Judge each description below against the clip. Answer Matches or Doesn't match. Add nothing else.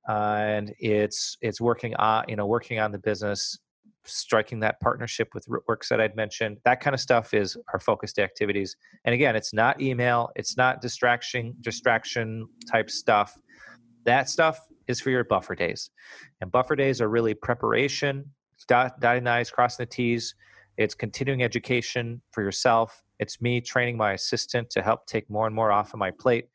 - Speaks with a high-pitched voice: Doesn't match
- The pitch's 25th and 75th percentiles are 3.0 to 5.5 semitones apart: Doesn't match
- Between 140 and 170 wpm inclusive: Doesn't match